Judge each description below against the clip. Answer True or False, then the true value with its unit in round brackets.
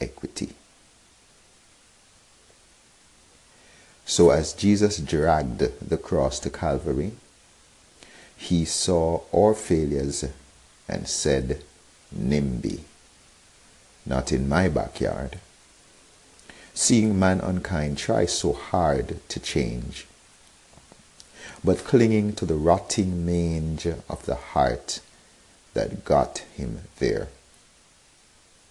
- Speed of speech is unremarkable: False (85 wpm)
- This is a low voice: True (80 Hz)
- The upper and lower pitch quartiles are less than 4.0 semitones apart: False (4.4 semitones)